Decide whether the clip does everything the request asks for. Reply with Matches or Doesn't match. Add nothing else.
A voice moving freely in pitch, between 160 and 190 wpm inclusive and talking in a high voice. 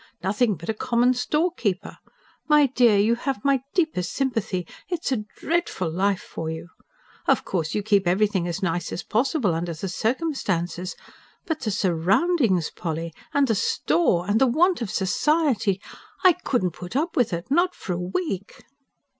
Matches